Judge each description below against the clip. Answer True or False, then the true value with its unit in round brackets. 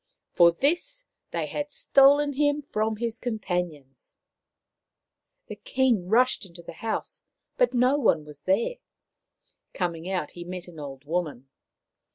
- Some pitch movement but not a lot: False (7.6 semitones)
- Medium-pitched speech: False (205 Hz)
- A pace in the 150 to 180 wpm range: False (135 wpm)